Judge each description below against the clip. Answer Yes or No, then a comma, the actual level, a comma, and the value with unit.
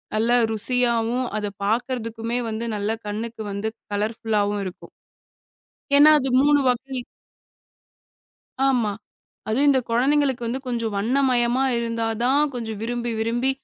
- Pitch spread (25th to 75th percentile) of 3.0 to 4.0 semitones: No, narrow, 2.4 semitones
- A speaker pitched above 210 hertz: Yes, high, 235 Hz